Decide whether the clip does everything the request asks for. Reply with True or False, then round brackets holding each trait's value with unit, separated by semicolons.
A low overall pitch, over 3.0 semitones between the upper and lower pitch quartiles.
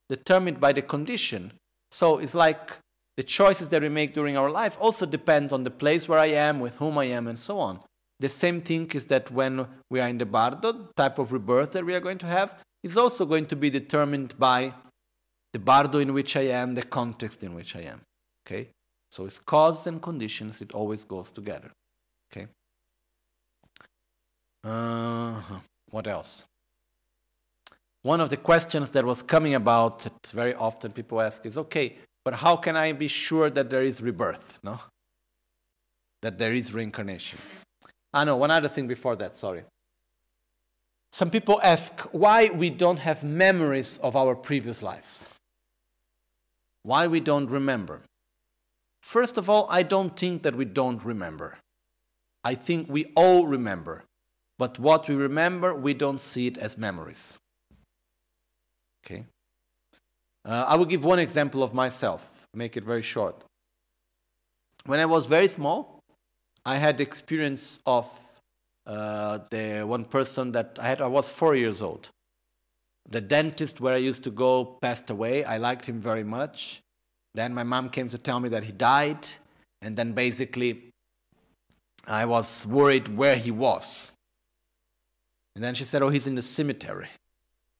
True (130 Hz; 5.0 semitones)